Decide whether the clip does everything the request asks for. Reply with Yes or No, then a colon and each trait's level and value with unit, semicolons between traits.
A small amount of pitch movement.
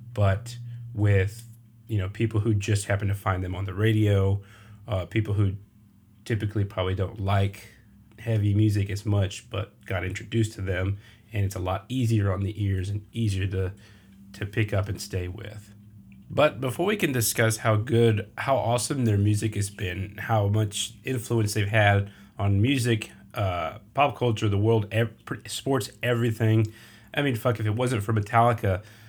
Yes: narrow, 2.3 semitones